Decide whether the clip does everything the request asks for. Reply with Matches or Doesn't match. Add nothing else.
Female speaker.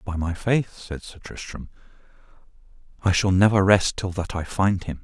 Doesn't match